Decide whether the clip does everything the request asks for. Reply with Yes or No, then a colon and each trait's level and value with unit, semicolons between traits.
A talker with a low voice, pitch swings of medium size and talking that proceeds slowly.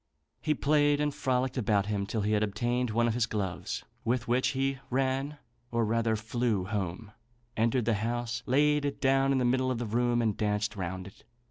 No: low, 120 Hz; average, 3.6 semitones; average, 200 wpm